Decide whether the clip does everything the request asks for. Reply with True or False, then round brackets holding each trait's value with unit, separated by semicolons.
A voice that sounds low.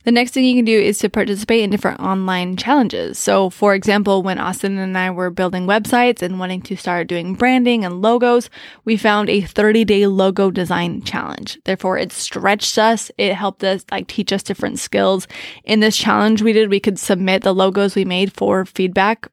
False (200 Hz)